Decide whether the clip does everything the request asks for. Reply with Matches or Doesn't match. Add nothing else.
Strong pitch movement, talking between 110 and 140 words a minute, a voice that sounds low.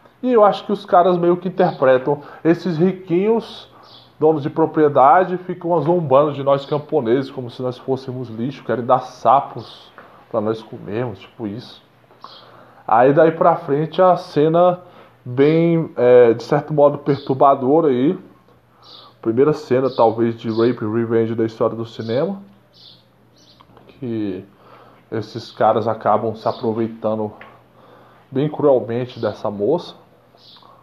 Matches